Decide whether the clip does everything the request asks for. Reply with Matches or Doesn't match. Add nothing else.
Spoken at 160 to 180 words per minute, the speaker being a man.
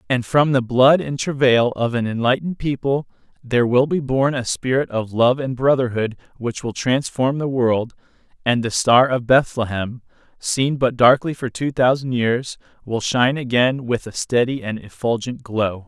Matches